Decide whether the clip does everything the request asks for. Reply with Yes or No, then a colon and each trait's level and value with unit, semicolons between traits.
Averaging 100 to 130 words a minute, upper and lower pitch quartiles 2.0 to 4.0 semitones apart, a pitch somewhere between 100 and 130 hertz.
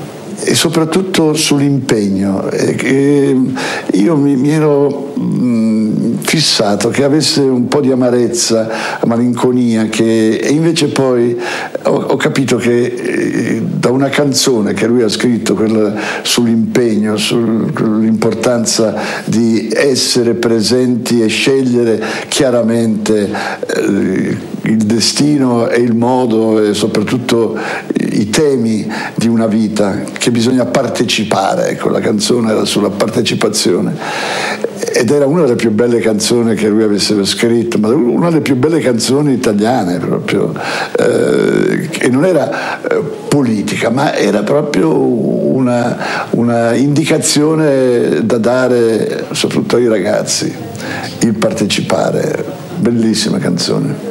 Yes: slow, 115 wpm; average, 3.5 semitones; low, 120 Hz